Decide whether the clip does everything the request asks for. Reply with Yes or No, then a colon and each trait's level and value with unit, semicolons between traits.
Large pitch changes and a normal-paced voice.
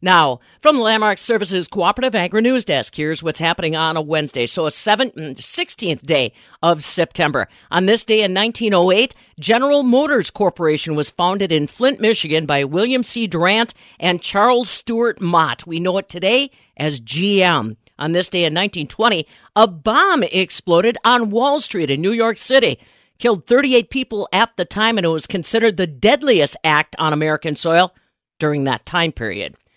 Yes: wide, 6.3 semitones; average, 170 wpm